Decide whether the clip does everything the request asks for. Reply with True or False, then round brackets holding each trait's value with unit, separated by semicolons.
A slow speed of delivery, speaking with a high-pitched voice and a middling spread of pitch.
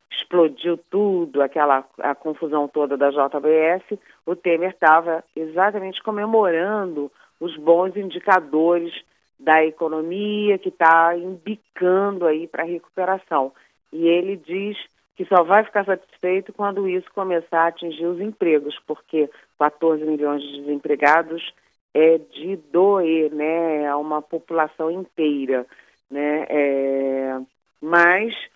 False (115 wpm; 165 Hz; 3.5 semitones)